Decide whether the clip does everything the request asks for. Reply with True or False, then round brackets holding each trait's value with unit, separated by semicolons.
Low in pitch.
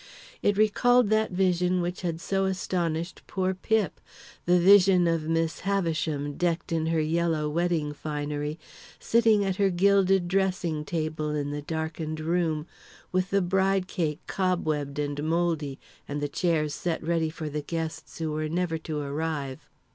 False (165 Hz)